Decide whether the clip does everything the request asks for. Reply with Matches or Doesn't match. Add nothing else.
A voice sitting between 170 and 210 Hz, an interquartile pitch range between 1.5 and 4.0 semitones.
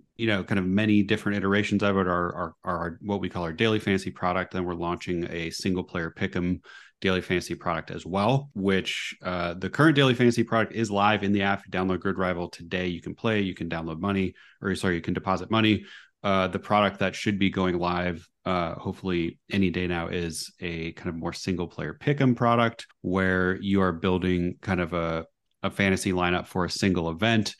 Doesn't match